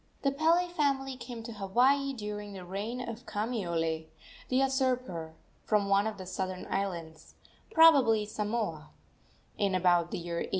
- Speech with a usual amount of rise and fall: No, wide, 5.7 semitones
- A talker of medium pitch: No, high, 210 Hz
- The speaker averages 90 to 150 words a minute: Yes, average, 145 wpm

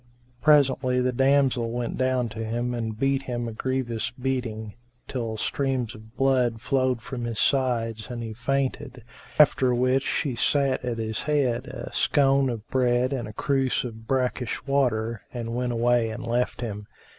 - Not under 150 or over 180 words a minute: Yes, average, 165 wpm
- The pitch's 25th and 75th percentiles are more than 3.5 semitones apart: No, narrow, 2.5 semitones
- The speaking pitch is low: Yes, low, 125 Hz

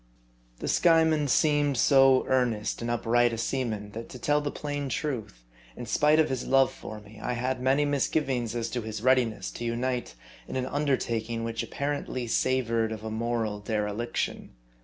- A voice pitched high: No, low, 125 Hz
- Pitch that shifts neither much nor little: Yes, average, 3.3 semitones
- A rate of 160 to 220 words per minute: Yes, average, 175 wpm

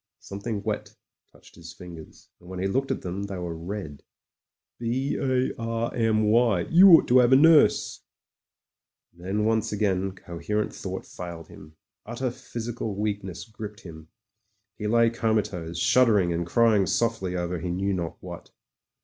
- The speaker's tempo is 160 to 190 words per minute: Yes, average, 170 wpm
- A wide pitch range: No, average, 4.5 semitones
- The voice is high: No, low, 105 Hz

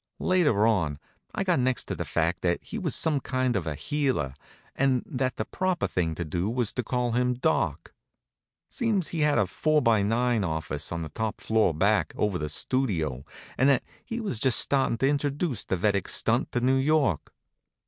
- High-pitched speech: No, low, 120 Hz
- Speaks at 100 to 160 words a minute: No, average, 195 wpm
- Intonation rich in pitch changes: Yes, wide, 7.3 semitones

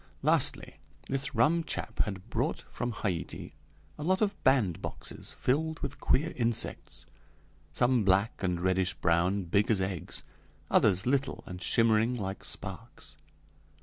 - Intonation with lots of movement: Yes, wide, 5.9 semitones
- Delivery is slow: Yes, slow, 130 wpm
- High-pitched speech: No, low, 110 Hz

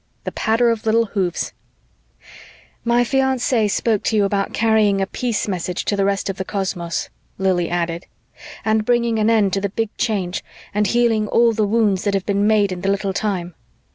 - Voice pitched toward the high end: Yes, high, 205 Hz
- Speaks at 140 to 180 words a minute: No, average, 190 wpm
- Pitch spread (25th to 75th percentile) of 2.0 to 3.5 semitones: Yes, average, 2.7 semitones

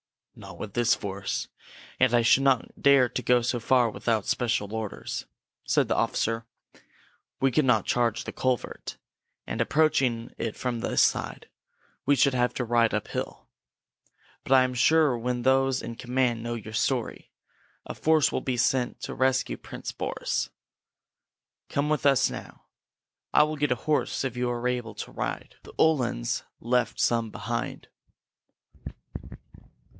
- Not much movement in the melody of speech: Yes, narrow, 2.3 semitones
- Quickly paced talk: No, average, 160 wpm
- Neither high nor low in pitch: No, low, 125 Hz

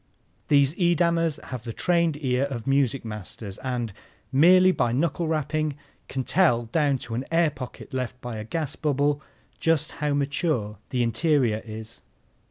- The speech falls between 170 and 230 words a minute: No, average, 155 wpm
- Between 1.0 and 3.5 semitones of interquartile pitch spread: No, average, 4.7 semitones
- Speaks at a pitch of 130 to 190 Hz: Yes, medium, 140 Hz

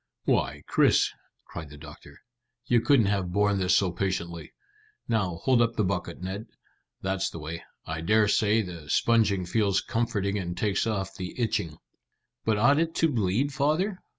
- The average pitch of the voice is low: Yes, low, 100 Hz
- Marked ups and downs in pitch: No, average, 4.3 semitones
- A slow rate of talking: No, average, 165 wpm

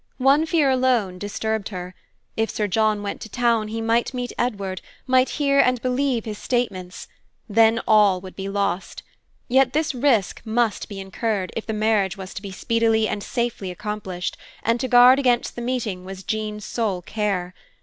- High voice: Yes, high, 220 Hz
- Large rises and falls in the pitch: No, average, 3.7 semitones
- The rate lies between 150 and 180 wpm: Yes, average, 175 wpm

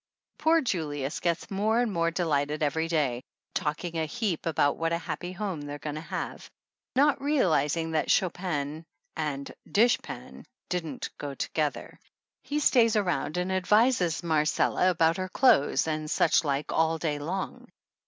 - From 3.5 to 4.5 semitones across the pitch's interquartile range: Yes, average, 4.0 semitones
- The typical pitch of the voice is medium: Yes, medium, 165 Hz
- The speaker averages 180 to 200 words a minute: No, average, 155 wpm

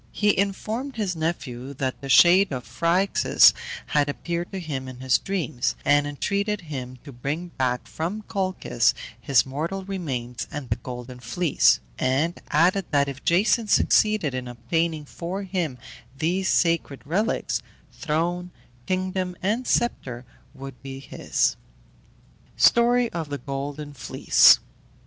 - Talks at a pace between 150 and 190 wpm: No, slow, 135 wpm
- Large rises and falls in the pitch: Yes, wide, 5.9 semitones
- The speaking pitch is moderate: Yes, medium, 160 Hz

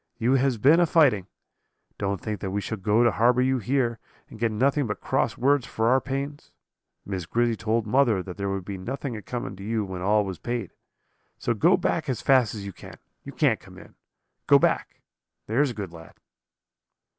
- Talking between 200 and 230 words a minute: Yes, fast, 205 wpm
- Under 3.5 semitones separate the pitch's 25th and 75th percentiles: No, average, 4.7 semitones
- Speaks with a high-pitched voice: No, low, 115 Hz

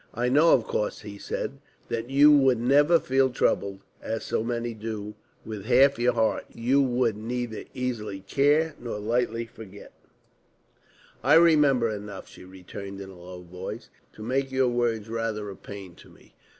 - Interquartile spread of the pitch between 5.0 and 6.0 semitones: No, average, 3.9 semitones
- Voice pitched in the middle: No, low, 115 Hz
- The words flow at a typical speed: Yes, average, 165 wpm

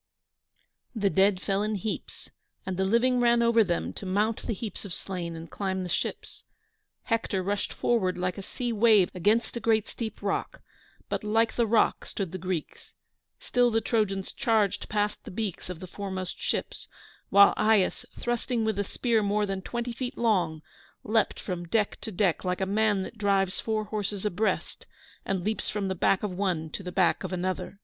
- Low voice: No, high, 205 Hz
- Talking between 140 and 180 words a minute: No, average, 190 wpm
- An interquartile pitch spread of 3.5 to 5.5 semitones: No, average, 2.9 semitones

